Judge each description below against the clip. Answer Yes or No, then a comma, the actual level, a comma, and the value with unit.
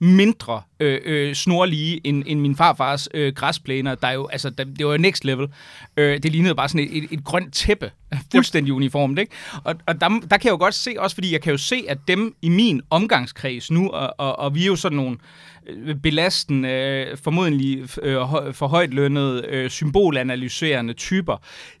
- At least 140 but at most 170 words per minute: No, average, 195 wpm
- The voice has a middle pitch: Yes, medium, 145 Hz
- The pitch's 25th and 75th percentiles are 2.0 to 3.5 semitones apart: No, average, 4.1 semitones